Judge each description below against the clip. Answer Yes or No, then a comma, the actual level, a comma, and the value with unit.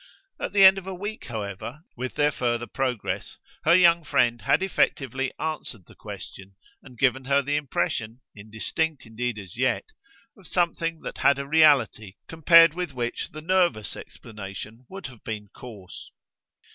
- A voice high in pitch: No, low, 135 Hz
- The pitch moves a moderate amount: No, wide, 6.4 semitones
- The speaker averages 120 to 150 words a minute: No, average, 160 wpm